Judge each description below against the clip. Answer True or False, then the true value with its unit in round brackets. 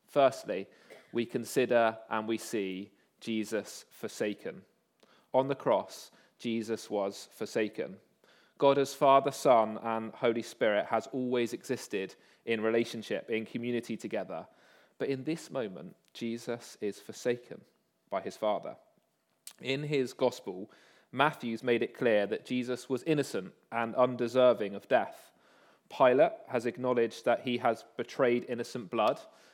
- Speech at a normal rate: False (130 wpm)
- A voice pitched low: True (120 Hz)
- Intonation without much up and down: True (2.0 semitones)